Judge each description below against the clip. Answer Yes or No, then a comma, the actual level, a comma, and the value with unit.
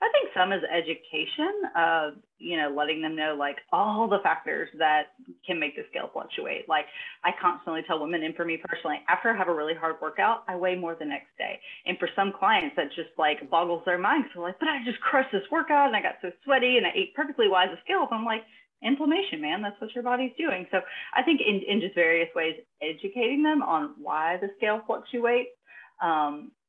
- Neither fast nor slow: No, fast, 220 wpm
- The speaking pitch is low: No, high, 195 Hz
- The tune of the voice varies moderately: No, wide, 7.7 semitones